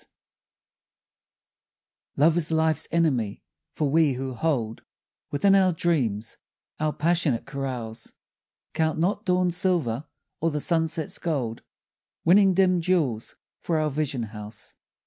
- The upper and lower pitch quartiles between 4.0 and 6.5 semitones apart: Yes, average, 5.1 semitones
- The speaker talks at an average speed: No, slow, 120 wpm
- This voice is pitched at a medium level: Yes, medium, 155 Hz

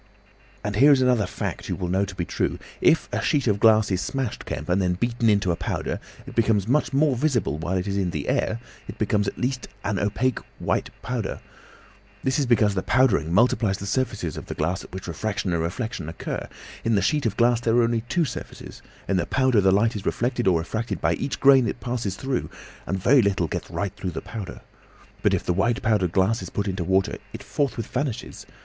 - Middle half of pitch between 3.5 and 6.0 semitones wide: Yes, average, 4.5 semitones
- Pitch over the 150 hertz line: No, low, 105 Hz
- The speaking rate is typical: No, fast, 220 wpm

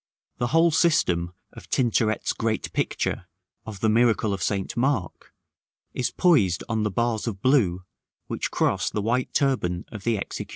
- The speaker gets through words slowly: No, average, 160 wpm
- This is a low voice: Yes, low, 110 Hz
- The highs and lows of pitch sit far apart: No, average, 4.3 semitones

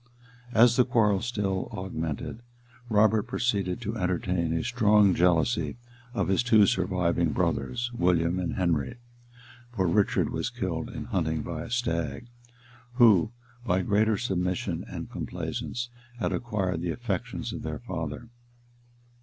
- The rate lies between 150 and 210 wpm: No, slow, 135 wpm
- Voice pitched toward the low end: Yes, very low, 95 Hz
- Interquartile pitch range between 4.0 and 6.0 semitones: Yes, average, 4.7 semitones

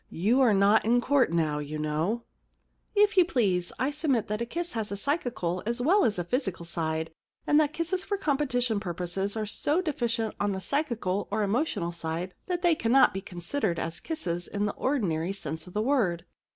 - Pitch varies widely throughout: Yes, wide, 8.0 semitones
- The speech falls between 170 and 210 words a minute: Yes, average, 200 wpm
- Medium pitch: No, high, 215 Hz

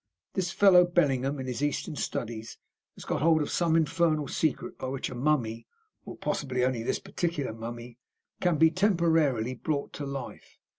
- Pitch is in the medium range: Yes, medium, 145 Hz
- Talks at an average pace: Yes, average, 165 wpm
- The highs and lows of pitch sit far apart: No, average, 4.7 semitones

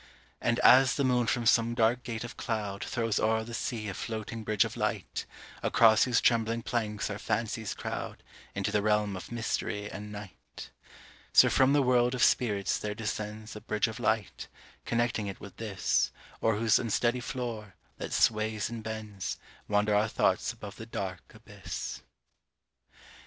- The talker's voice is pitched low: Yes, low, 110 Hz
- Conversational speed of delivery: Yes, average, 165 wpm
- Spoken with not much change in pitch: Yes, narrow, 2.1 semitones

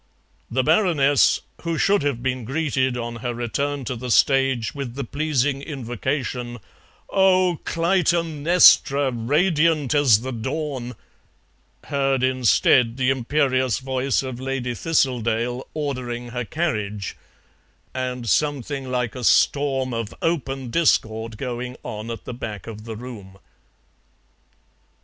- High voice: No, low, 130 Hz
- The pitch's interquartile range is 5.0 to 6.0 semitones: No, average, 3.2 semitones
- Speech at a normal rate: No, slow, 120 wpm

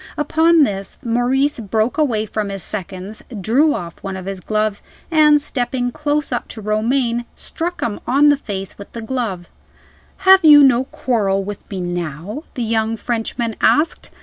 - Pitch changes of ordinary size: No, wide, 5.9 semitones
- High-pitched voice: Yes, high, 230 Hz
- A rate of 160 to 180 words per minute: Yes, average, 165 wpm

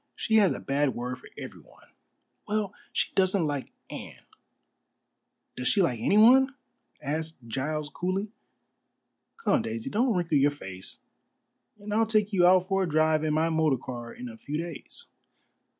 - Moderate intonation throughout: No, wide, 6.3 semitones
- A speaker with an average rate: Yes, average, 155 wpm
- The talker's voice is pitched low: No, medium, 160 Hz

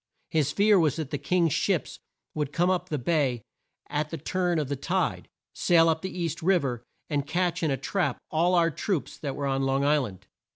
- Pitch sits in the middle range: Yes, medium, 155 Hz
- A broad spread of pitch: No, average, 3.8 semitones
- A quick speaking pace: Yes, fast, 215 wpm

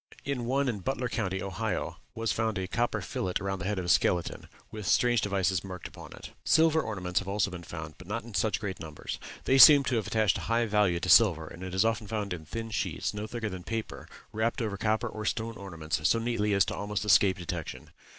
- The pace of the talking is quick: Yes, fast, 230 wpm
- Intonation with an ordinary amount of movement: Yes, average, 3.6 semitones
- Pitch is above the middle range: No, low, 105 Hz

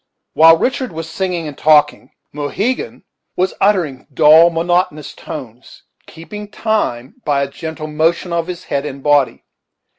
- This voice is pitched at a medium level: Yes, medium, 160 Hz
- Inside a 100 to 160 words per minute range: Yes, average, 140 wpm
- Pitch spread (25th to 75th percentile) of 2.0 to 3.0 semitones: No, average, 3.6 semitones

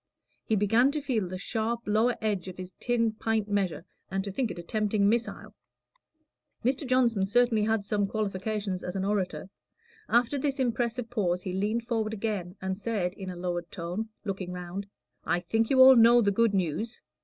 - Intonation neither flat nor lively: Yes, average, 3.5 semitones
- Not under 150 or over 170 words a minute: No, average, 185 wpm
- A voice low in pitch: No, high, 210 Hz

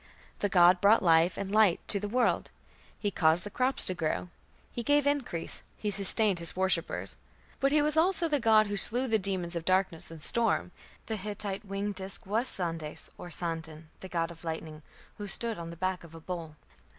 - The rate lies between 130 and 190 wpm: No, average, 200 wpm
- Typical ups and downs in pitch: Yes, average, 4.5 semitones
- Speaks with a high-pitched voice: Yes, high, 195 Hz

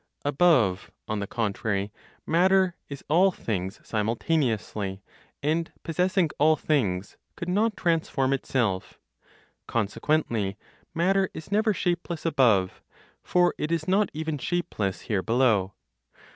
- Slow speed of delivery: Yes, slow, 115 wpm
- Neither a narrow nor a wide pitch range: No, wide, 8.5 semitones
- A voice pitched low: No, medium, 145 Hz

